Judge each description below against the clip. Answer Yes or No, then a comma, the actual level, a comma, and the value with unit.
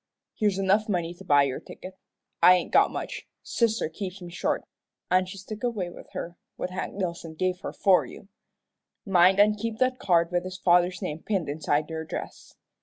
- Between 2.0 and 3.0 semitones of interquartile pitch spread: Yes, narrow, 2.5 semitones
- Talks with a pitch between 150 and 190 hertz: Yes, medium, 185 Hz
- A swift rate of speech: No, average, 190 wpm